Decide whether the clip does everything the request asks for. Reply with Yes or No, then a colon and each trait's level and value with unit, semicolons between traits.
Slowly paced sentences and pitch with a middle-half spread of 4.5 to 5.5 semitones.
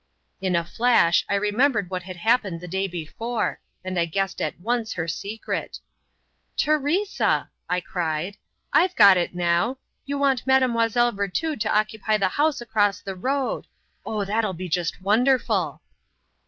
No: average, 150 wpm; average, 5.0 semitones